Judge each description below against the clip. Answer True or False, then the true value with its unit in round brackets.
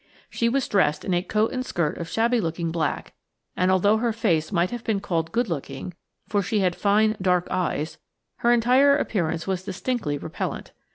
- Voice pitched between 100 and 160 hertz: False (190 Hz)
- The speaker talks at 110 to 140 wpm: False (175 wpm)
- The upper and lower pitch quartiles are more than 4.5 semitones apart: True (5.1 semitones)